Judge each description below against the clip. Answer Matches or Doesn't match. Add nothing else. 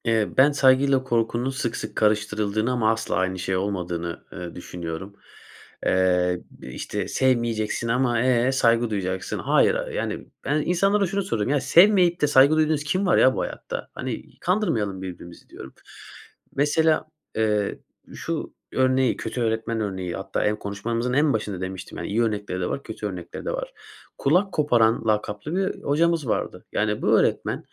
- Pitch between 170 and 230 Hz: Doesn't match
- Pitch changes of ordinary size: Doesn't match